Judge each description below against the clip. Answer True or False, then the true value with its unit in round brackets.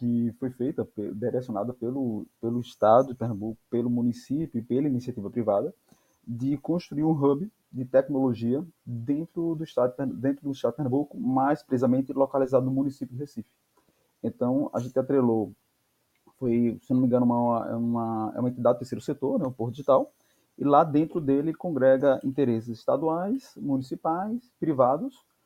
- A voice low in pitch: True (130 Hz)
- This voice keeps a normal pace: True (160 wpm)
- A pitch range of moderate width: True (3.4 semitones)